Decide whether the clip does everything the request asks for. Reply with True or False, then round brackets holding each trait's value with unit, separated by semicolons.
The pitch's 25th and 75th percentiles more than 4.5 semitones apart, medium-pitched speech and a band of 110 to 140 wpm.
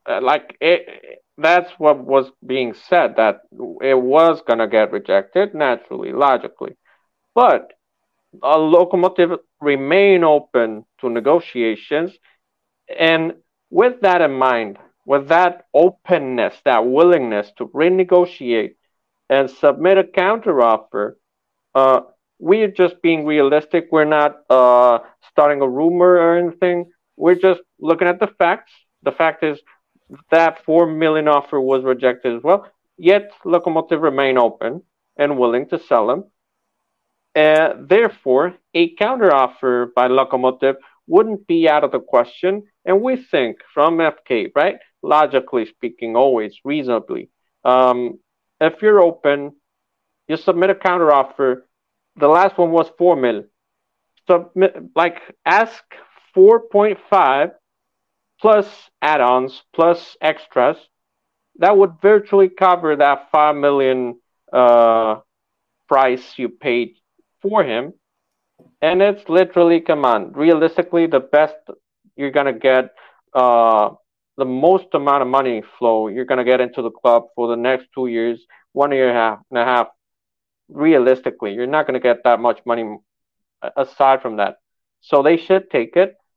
True (5.5 semitones; 150 Hz; 135 wpm)